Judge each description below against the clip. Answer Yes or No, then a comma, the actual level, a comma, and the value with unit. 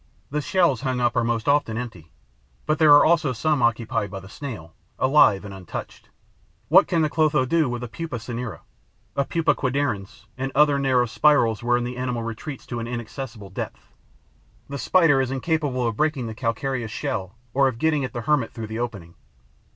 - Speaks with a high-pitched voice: No, low, 125 Hz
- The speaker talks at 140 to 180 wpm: No, average, 190 wpm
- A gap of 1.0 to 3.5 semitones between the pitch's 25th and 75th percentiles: No, average, 4.3 semitones